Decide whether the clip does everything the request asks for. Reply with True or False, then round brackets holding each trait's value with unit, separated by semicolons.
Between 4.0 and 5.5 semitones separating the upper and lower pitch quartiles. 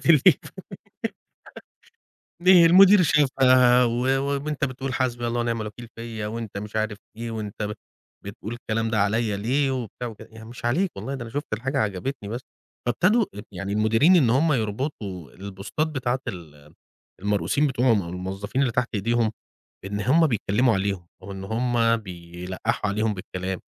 True (4.4 semitones)